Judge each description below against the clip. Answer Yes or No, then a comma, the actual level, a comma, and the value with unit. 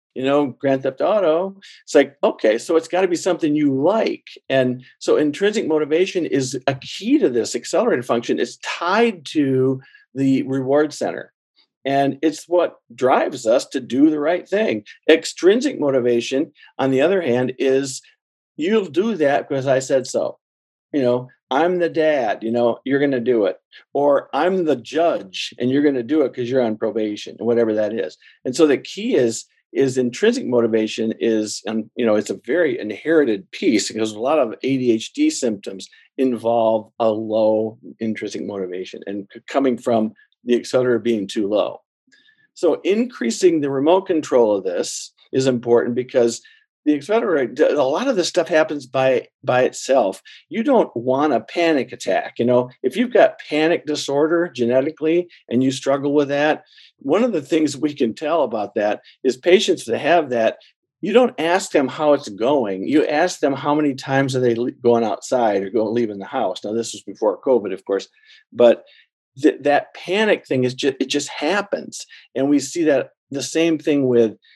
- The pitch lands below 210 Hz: Yes, medium, 140 Hz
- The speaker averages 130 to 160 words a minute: No, average, 180 wpm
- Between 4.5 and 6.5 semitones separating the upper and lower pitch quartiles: Yes, wide, 5.5 semitones